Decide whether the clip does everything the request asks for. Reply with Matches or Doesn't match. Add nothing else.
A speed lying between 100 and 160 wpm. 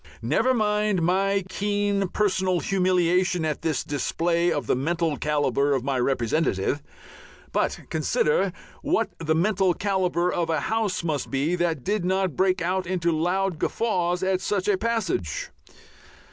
Matches